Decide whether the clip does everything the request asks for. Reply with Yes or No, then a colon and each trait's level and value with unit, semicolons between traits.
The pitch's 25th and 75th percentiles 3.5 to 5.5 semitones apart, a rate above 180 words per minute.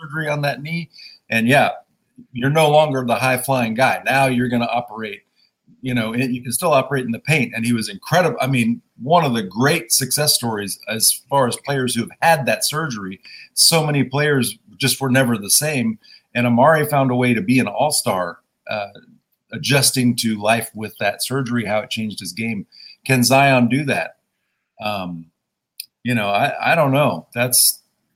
No: average, 3.1 semitones; average, 190 wpm